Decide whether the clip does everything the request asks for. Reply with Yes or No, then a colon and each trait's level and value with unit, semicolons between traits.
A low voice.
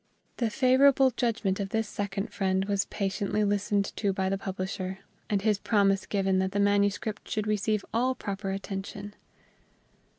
No: high, 200 Hz